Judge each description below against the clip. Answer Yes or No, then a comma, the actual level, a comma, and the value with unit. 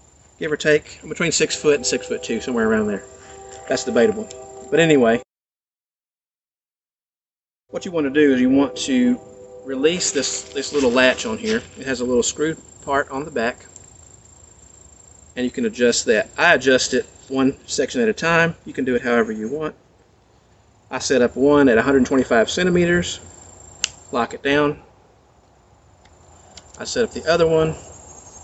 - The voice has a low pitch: Yes, low, 130 Hz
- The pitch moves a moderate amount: No, wide, 6.9 semitones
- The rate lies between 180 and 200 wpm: No, average, 165 wpm